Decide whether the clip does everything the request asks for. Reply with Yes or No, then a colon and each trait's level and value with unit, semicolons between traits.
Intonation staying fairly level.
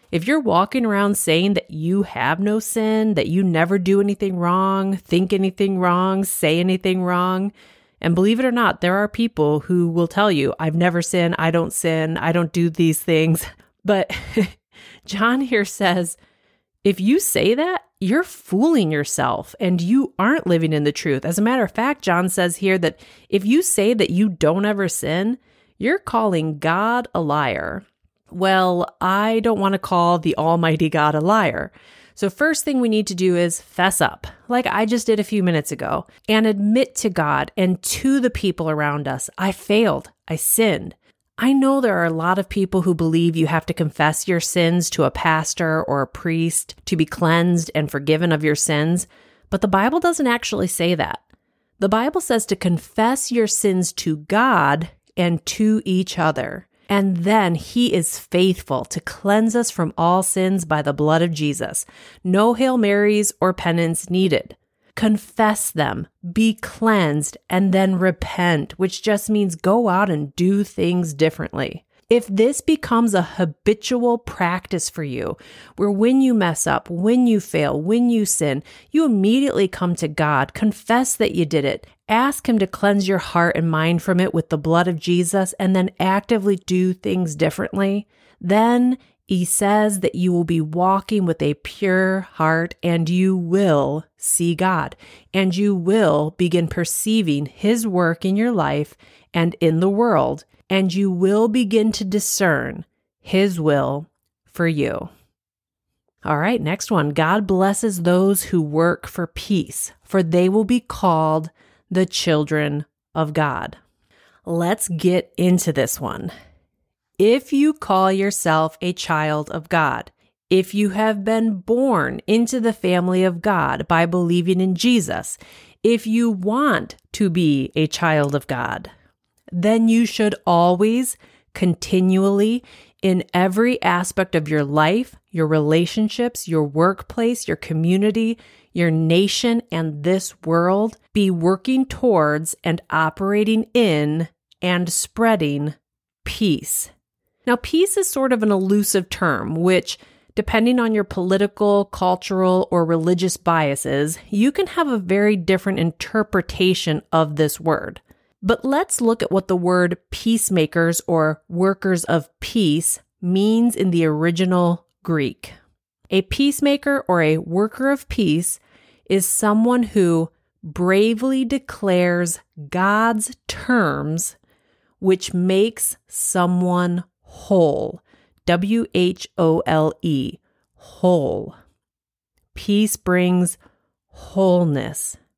No: average, 4.3 semitones